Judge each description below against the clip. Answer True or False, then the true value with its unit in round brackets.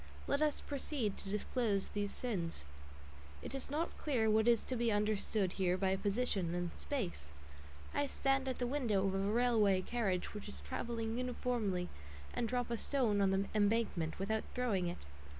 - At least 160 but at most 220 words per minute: True (170 wpm)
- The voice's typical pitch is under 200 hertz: False (215 Hz)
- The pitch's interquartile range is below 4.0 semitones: False (4.3 semitones)